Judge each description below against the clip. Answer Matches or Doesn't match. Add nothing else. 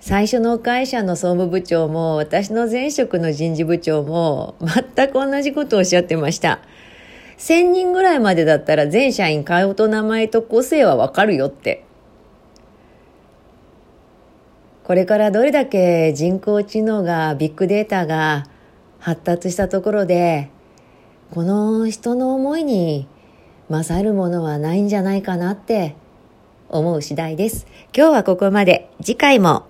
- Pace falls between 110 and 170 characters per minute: Doesn't match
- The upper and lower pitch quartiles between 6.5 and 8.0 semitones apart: Doesn't match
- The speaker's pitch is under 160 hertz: Doesn't match